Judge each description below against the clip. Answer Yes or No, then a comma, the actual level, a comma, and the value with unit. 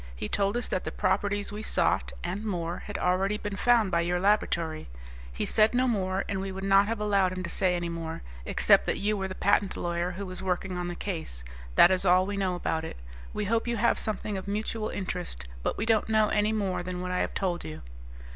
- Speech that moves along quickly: Yes, fast, 235 wpm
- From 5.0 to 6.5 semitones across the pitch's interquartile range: No, average, 2.7 semitones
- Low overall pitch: No, high, 190 Hz